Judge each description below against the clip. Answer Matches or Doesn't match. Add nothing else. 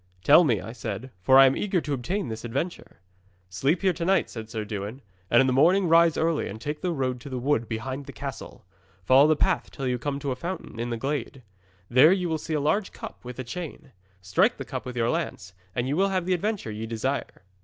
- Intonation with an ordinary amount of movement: Doesn't match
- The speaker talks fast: Matches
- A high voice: Doesn't match